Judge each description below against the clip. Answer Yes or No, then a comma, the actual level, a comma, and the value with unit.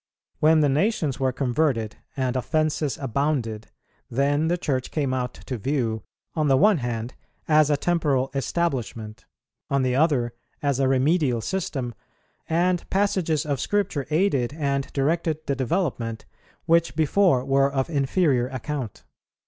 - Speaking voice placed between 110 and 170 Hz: Yes, medium, 140 Hz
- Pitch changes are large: No, average, 3.8 semitones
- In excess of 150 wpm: No, average, 140 wpm